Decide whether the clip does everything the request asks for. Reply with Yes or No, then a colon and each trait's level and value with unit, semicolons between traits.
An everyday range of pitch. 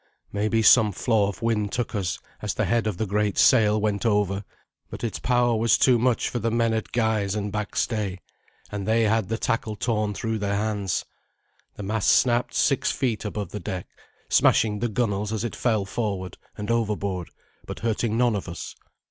No: narrow, 2.1 semitones